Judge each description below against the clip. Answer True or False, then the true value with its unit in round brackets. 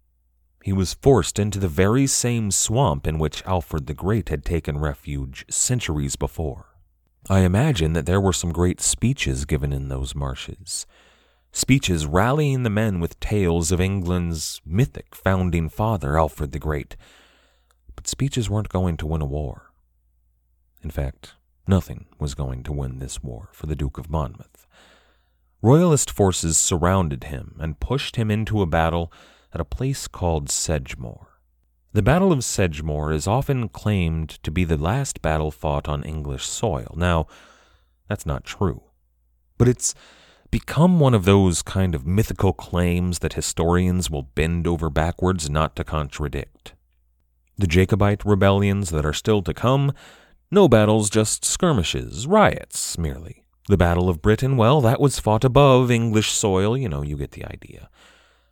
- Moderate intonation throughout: False (5.8 semitones)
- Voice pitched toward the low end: True (85 Hz)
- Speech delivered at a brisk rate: False (155 wpm)